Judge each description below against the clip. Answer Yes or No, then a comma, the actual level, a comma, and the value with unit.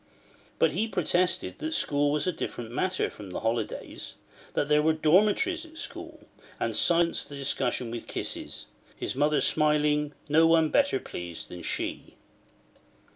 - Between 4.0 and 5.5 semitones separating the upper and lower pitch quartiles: Yes, average, 4.5 semitones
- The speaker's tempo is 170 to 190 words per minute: No, average, 150 wpm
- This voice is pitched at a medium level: Yes, medium, 150 Hz